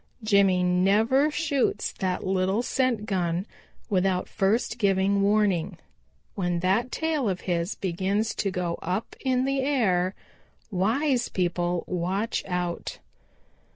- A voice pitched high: Yes, high, 195 Hz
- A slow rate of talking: Yes, slow, 120 wpm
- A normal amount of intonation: Yes, average, 4.1 semitones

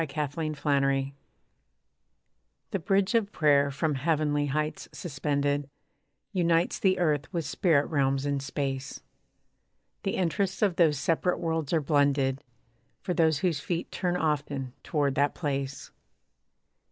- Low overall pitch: No, medium, 150 Hz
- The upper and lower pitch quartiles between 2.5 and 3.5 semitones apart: Yes, average, 3.1 semitones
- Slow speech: Yes, slow, 130 wpm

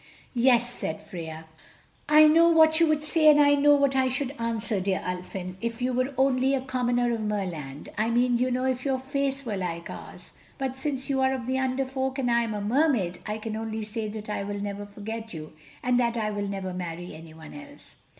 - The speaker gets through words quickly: Yes, fast, 220 wpm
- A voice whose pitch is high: Yes, high, 240 Hz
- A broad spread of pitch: No, average, 4.6 semitones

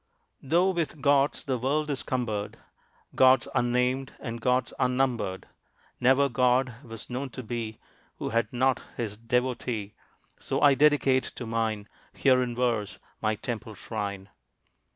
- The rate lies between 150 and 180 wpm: No, slow, 135 wpm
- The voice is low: Yes, low, 125 Hz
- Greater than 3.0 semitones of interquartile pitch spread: No, narrow, 2.6 semitones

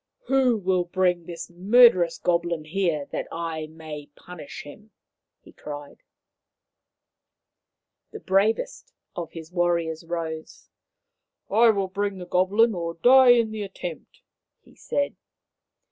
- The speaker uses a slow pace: Yes, slow, 130 wpm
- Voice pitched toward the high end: No, medium, 180 Hz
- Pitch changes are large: No, average, 3.9 semitones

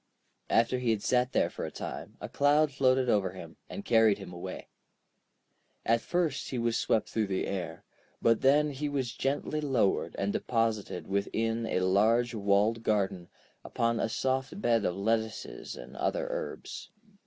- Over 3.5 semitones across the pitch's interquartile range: Yes, average, 4.6 semitones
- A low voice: Yes, low, 115 Hz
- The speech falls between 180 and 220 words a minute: No, average, 165 wpm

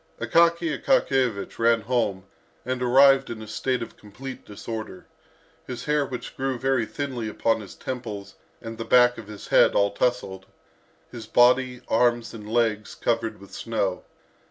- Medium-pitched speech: No, low, 120 Hz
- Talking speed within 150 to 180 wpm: Yes, average, 155 wpm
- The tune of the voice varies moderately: Yes, average, 3.0 semitones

